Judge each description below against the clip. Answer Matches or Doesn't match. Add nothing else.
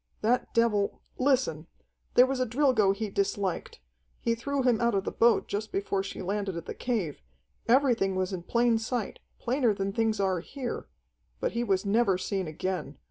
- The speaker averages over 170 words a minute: Matches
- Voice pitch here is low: Doesn't match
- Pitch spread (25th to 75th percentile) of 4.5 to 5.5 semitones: Doesn't match